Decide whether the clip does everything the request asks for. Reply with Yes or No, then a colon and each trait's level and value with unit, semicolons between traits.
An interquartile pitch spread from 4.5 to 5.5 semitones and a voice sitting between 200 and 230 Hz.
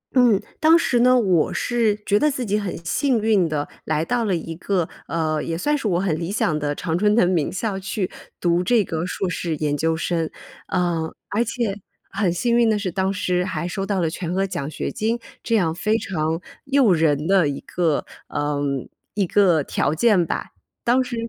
No: average, 5.0 semitones; medium, 185 Hz